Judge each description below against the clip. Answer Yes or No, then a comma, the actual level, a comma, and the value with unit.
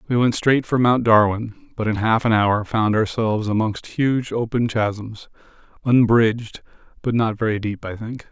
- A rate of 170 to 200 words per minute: Yes, average, 175 wpm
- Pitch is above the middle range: No, low, 110 Hz